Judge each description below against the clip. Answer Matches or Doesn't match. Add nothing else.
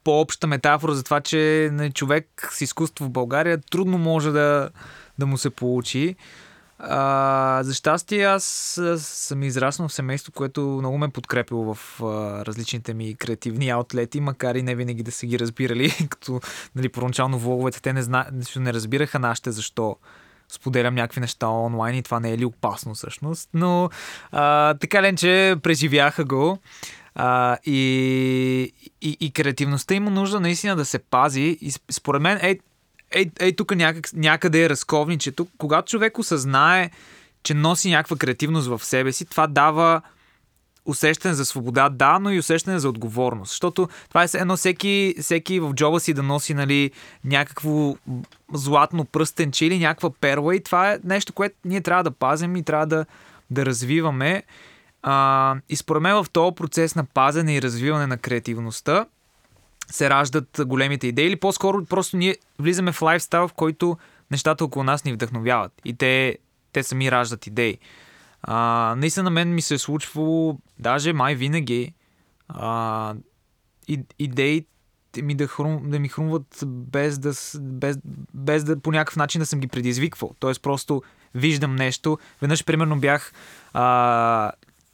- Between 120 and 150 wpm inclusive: Doesn't match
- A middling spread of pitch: Matches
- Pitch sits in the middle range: Matches